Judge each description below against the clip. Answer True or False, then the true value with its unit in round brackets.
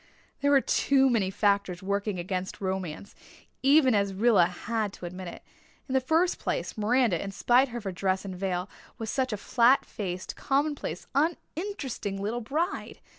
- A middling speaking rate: True (160 wpm)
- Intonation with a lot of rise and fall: True (5.7 semitones)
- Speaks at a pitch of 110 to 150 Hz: False (210 Hz)